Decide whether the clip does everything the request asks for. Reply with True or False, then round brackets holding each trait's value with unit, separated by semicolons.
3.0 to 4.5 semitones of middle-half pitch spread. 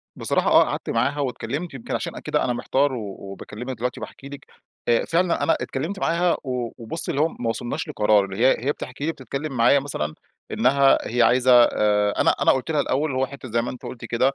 True (3.4 semitones)